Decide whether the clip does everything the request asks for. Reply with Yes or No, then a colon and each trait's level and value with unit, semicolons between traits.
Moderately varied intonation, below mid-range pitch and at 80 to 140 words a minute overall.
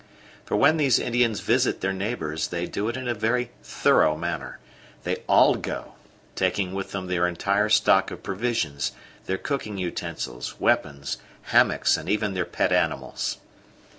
No: average, 4.9 semitones; low, 100 Hz; average, 155 wpm